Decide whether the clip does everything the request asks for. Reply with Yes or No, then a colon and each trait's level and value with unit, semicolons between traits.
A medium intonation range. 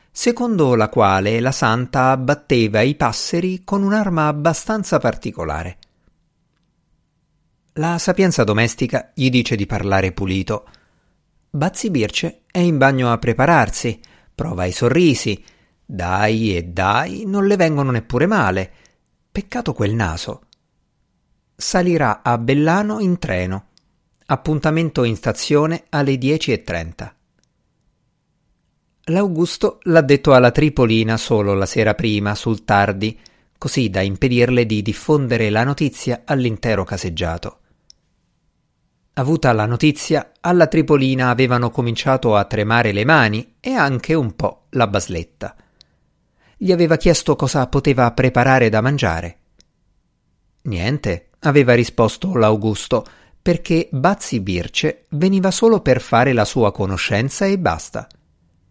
No: wide, 6.6 semitones